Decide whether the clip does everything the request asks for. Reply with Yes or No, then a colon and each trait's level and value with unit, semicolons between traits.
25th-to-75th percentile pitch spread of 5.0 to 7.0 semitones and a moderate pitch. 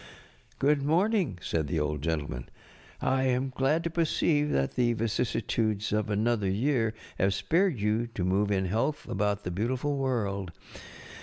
No: wide, 5.5 semitones; low, 115 Hz